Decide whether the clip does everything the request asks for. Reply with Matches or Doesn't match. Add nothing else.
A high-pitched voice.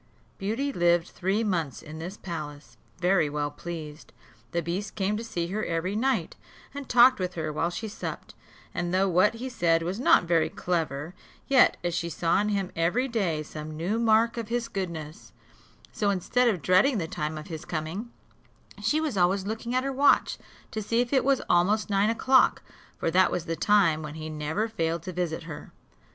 Doesn't match